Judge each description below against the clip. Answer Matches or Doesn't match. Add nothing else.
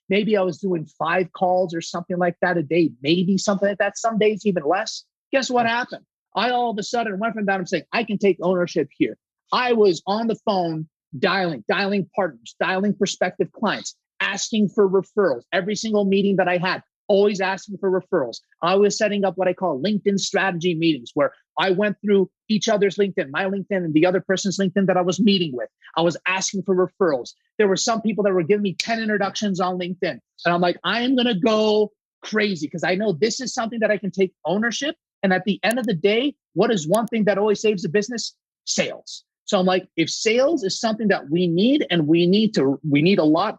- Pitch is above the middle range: Matches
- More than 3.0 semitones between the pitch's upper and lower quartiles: Doesn't match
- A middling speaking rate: Doesn't match